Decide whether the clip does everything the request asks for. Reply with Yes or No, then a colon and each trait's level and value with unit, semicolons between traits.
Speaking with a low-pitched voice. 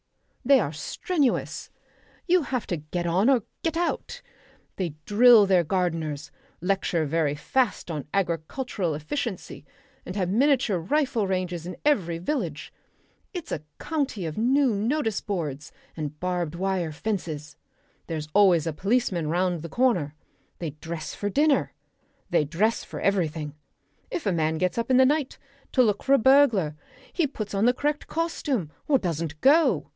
No: high, 190 Hz